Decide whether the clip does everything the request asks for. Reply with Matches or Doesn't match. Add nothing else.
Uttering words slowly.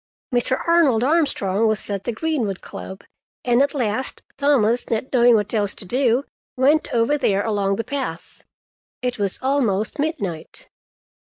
Doesn't match